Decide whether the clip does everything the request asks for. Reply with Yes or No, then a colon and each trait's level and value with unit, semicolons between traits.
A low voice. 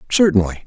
Yes: low, 125 Hz